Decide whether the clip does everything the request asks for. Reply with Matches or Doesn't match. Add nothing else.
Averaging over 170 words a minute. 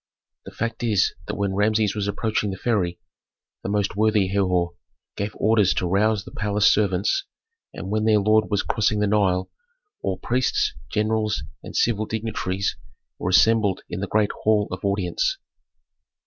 Doesn't match